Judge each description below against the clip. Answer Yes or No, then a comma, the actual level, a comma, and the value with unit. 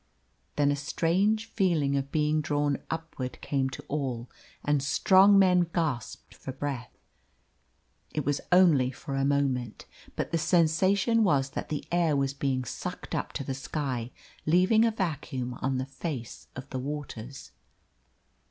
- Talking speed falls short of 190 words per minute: Yes, average, 150 wpm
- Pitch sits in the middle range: Yes, medium, 145 Hz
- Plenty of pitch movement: No, average, 4.1 semitones